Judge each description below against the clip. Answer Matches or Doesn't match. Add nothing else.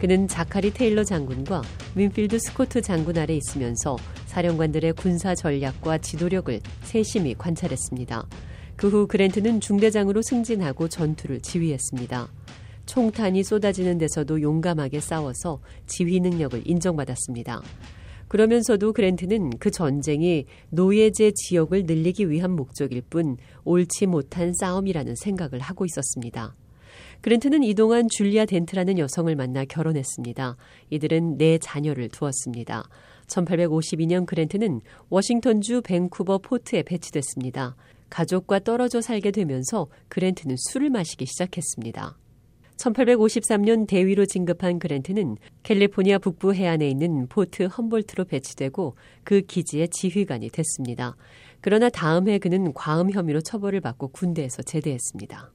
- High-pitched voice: Doesn't match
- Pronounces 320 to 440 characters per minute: Matches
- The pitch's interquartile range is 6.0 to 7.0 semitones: Matches